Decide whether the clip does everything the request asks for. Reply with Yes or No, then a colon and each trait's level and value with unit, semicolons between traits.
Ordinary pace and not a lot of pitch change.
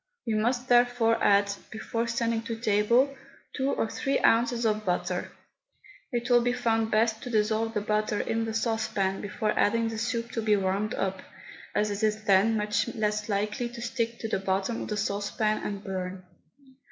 Yes: average, 180 wpm; narrow, 2.0 semitones